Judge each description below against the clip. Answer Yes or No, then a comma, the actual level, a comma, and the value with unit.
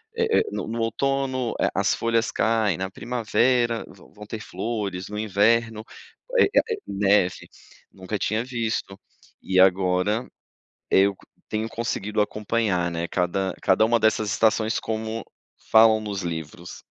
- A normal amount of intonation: Yes, average, 3.0 semitones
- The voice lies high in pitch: No, low, 110 Hz